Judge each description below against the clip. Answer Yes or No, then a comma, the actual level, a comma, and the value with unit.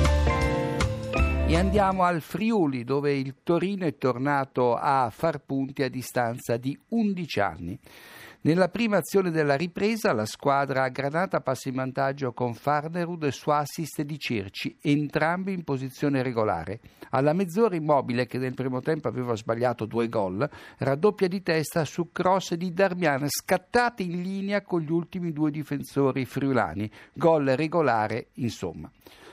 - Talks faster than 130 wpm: Yes, average, 145 wpm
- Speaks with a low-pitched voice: No, medium, 145 Hz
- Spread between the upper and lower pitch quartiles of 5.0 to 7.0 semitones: Yes, wide, 5.5 semitones